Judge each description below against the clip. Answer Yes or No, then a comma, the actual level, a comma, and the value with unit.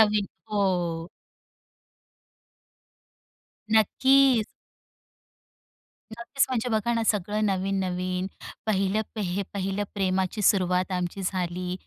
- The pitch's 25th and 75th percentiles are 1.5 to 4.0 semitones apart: Yes, average, 2.8 semitones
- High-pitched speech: Yes, high, 195 Hz